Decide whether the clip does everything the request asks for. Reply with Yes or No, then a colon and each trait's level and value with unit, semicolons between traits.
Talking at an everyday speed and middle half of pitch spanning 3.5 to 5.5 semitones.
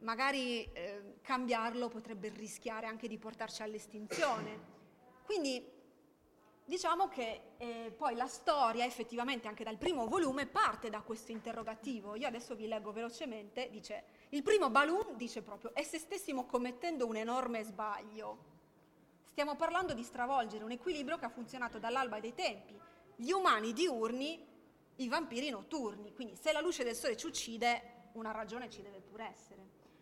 Yes: average, 150 wpm; average, 4.0 semitones